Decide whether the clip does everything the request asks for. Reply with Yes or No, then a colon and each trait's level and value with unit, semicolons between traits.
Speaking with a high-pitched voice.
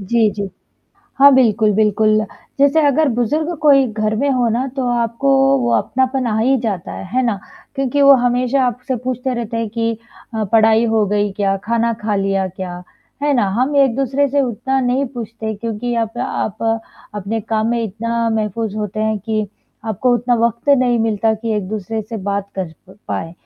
Yes: high, 230 Hz